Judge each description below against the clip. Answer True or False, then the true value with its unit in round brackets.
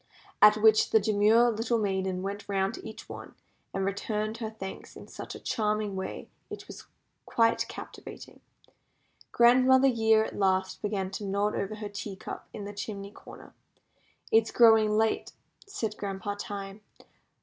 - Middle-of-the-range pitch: False (210 Hz)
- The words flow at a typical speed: True (155 wpm)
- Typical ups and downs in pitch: False (1.9 semitones)